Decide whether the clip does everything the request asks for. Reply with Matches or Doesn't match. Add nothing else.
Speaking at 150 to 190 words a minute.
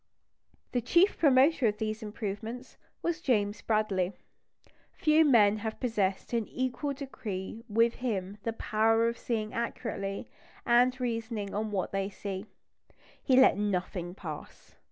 Doesn't match